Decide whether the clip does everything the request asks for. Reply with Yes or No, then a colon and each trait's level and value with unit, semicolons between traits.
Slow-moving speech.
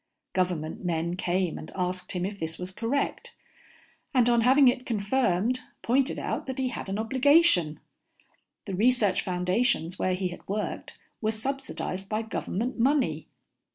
No: average, 150 wpm